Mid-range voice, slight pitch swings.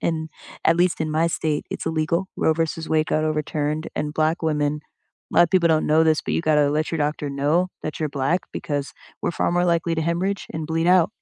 Yes: medium, 160 Hz; narrow, 1.7 semitones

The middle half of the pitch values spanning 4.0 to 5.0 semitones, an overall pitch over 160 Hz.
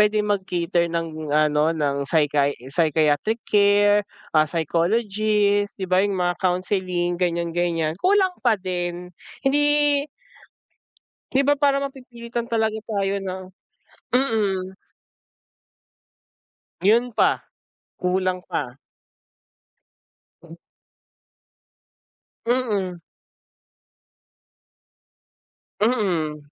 Yes: average, 4.5 semitones; high, 190 Hz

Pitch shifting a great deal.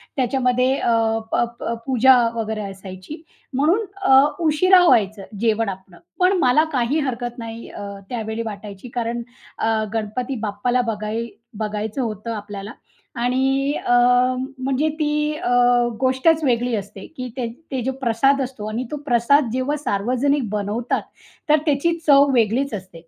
No: average, 3.9 semitones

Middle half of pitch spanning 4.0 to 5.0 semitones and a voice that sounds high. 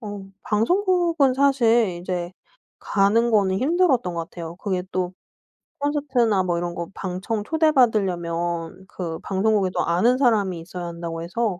No: wide, 5.6 semitones; high, 195 Hz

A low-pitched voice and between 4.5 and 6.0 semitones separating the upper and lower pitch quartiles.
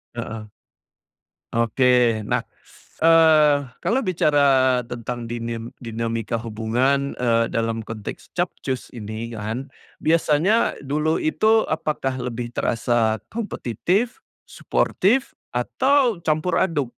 Yes: low, 125 Hz; wide, 5.5 semitones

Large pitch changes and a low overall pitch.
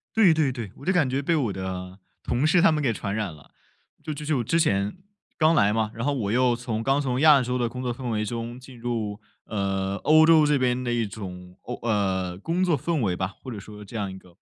Yes: wide, 5.9 semitones; low, 120 Hz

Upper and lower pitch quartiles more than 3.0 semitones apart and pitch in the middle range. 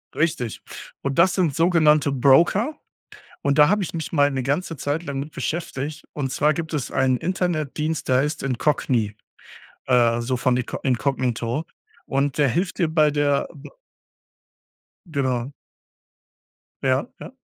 Yes: average, 3.5 semitones; medium, 145 Hz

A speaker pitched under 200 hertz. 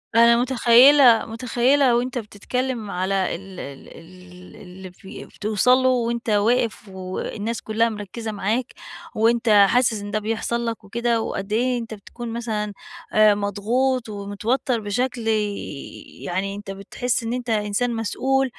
No: high, 225 Hz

